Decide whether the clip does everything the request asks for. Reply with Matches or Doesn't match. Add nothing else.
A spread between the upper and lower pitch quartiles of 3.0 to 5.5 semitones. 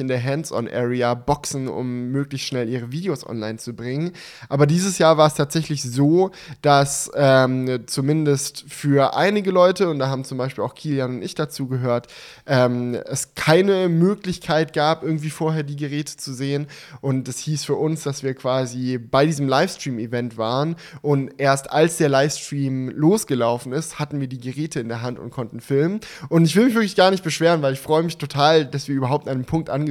Matches